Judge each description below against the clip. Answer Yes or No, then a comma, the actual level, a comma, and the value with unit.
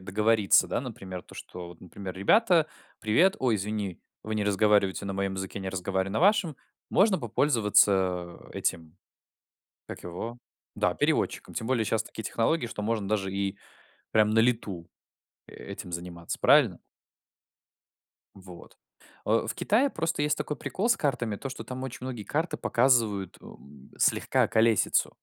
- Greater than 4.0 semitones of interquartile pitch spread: Yes, average, 4.9 semitones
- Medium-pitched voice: No, low, 105 Hz